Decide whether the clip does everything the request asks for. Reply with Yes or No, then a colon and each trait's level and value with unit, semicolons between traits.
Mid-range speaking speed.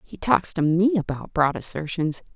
Yes: average, 180 wpm